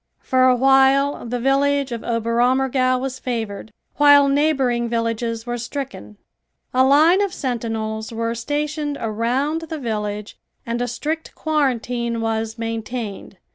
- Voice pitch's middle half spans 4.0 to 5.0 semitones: No, average, 3.4 semitones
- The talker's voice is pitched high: Yes, high, 245 Hz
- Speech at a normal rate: No, slow, 130 wpm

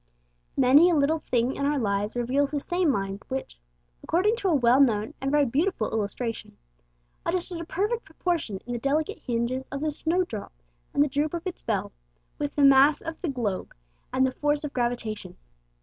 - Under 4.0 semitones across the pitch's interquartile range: No, average, 4.9 semitones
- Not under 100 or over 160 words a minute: No, average, 185 wpm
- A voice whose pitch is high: Yes, very high, 275 Hz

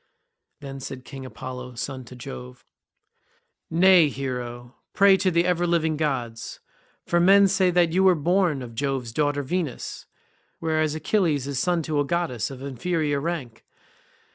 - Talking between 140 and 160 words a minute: Yes, average, 150 wpm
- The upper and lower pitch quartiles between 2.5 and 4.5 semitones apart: No, average, 5.1 semitones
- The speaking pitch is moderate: Yes, medium, 145 Hz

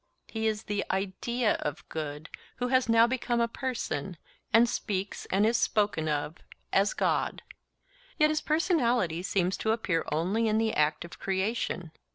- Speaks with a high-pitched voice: Yes, high, 215 Hz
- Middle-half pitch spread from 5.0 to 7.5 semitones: Yes, average, 5.3 semitones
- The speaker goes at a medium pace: Yes, average, 160 wpm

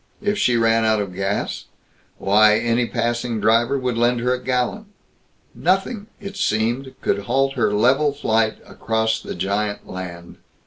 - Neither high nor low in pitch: No, low, 115 Hz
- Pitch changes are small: No, average, 3.4 semitones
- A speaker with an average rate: Yes, average, 150 wpm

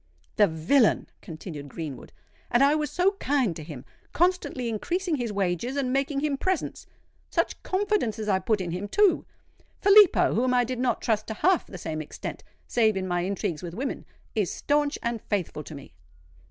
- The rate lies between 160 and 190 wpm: Yes, average, 170 wpm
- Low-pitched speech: No, high, 230 Hz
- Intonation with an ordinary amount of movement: No, wide, 8.0 semitones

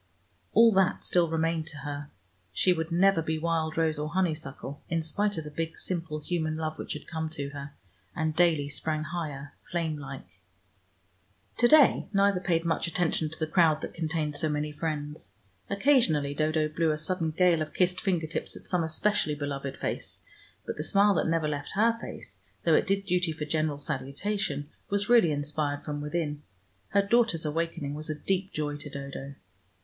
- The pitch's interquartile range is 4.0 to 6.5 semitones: No, average, 3.0 semitones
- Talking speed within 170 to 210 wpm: Yes, average, 185 wpm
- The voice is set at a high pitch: No, medium, 160 Hz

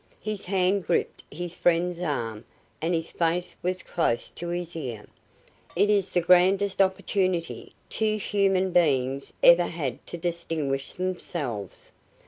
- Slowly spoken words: Yes, slow, 130 wpm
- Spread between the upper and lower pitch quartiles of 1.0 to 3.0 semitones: Yes, narrow, 2.6 semitones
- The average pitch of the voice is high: No, medium, 175 Hz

